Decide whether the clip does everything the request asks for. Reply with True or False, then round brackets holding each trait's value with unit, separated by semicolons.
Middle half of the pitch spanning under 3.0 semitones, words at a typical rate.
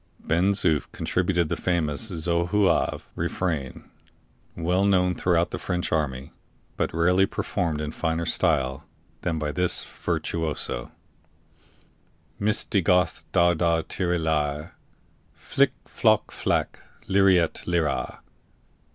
False (2.6 semitones; 110 wpm)